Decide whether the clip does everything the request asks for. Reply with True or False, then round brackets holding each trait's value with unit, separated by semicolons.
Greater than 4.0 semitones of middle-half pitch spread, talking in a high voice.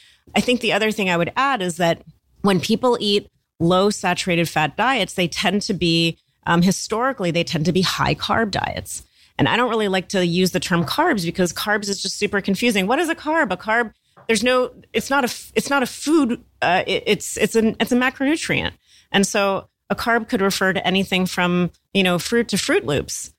True (4.6 semitones; 200 Hz)